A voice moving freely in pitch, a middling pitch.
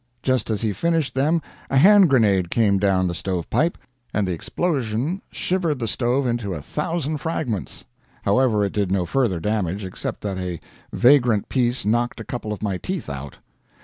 No: wide, 5.9 semitones; low, 115 Hz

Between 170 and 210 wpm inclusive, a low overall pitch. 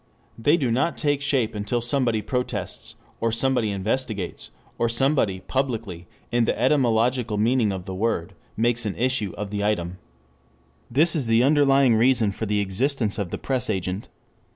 No: average, 155 wpm; low, 115 Hz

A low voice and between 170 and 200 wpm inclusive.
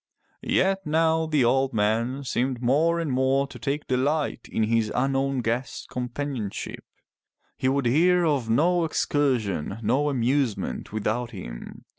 No: low, 130 Hz; slow, 135 wpm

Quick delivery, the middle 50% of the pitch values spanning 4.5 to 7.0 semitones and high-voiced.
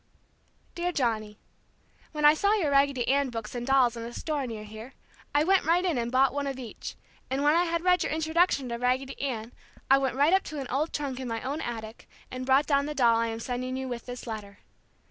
No: fast, 235 wpm; average, 3.8 semitones; very high, 265 Hz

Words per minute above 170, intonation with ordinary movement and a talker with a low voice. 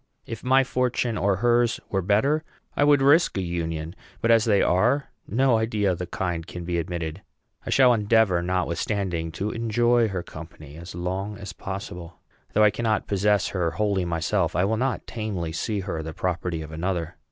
Yes: average, 185 wpm; average, 4.7 semitones; very low, 95 Hz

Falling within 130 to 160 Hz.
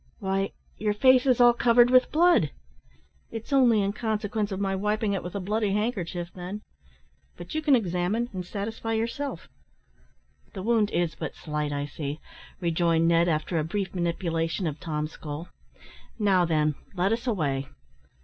No: high, 195 Hz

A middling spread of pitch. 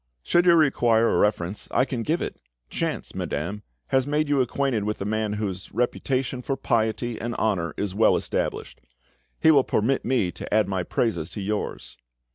Yes: average, 4.4 semitones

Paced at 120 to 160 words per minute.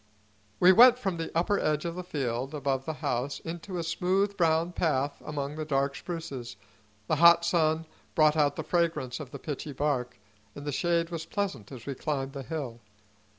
No: average, 190 wpm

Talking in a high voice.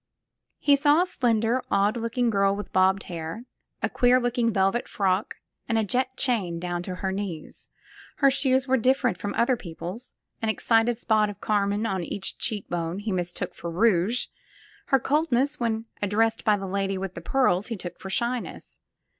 Yes: high, 215 Hz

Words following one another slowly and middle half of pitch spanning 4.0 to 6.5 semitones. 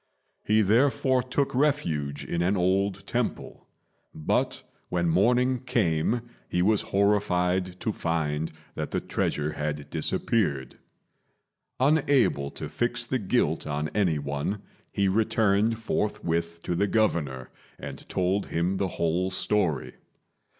Yes: slow, 120 wpm; average, 5.3 semitones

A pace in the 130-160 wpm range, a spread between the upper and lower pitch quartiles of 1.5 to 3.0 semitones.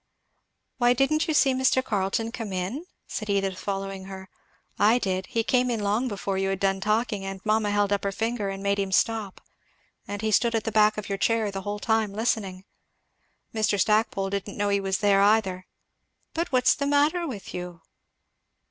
No: average, 190 wpm; average, 2.7 semitones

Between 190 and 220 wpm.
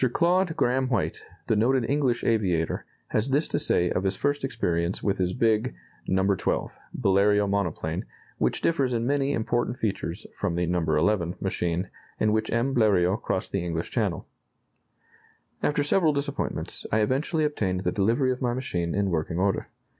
No: average, 165 wpm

